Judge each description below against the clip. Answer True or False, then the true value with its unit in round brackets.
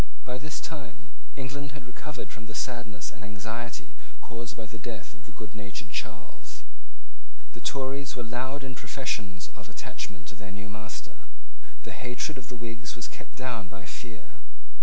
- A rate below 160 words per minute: False (165 wpm)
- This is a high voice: False (115 Hz)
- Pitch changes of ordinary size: True (3.8 semitones)